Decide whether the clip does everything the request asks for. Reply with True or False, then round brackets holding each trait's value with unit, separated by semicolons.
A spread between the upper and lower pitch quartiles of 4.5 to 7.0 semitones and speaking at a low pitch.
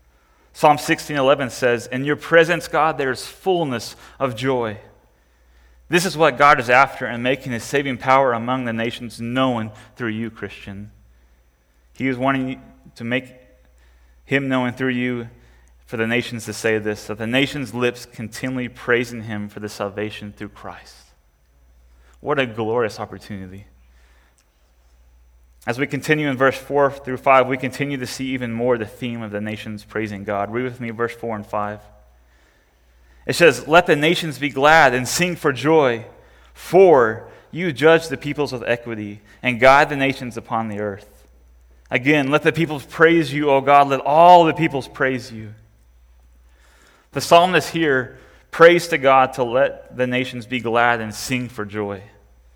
True (4.9 semitones; 120 Hz)